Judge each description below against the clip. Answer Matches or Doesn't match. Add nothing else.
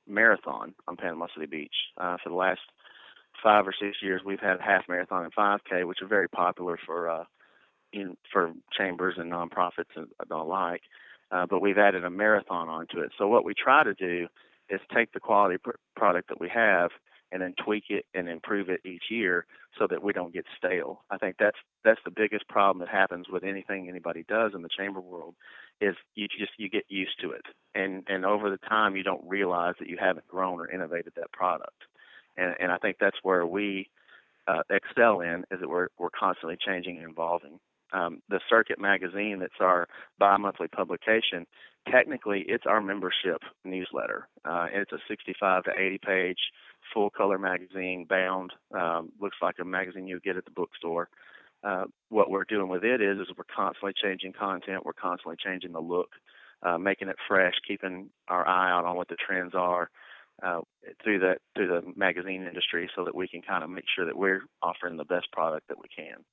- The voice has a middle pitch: Doesn't match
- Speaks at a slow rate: Doesn't match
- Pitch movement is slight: Matches